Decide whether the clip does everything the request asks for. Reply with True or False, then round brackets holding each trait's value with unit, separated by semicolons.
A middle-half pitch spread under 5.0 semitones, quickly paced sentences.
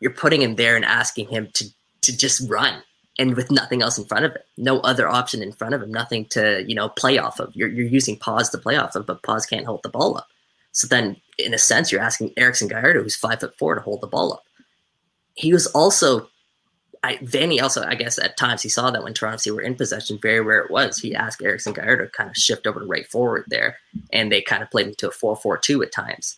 True (2.9 semitones; 255 wpm)